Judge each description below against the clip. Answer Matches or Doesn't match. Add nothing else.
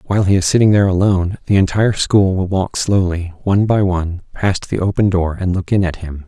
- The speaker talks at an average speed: Doesn't match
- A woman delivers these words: Doesn't match